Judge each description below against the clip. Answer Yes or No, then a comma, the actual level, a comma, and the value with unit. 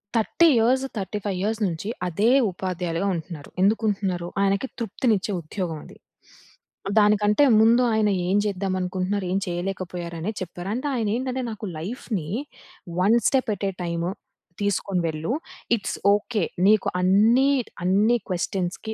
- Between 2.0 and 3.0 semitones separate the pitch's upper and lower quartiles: No, average, 3.4 semitones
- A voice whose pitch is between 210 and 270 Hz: No, high, 200 Hz